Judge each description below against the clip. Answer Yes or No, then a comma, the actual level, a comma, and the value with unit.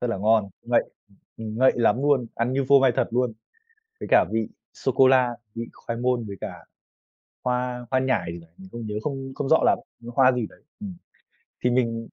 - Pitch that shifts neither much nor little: No, narrow, 2.3 semitones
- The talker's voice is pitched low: Yes, low, 125 Hz